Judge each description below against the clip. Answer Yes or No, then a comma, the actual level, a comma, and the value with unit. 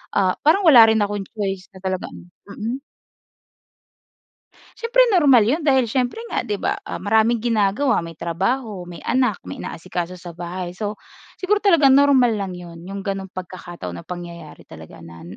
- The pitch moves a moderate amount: No, wide, 6.0 semitones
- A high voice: Yes, high, 200 Hz